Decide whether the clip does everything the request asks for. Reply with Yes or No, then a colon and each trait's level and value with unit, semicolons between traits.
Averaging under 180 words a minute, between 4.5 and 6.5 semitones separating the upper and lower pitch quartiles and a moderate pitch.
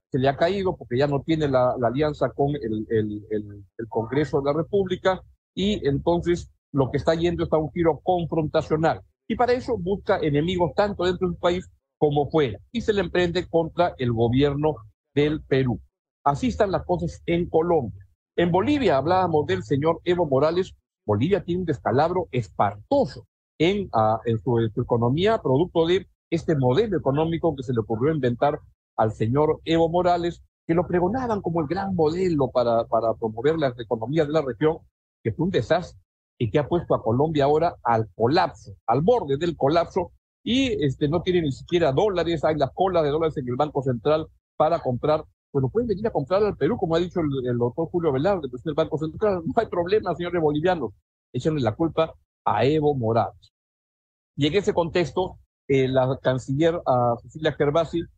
No: average, 185 wpm; average, 5.1 semitones; medium, 155 Hz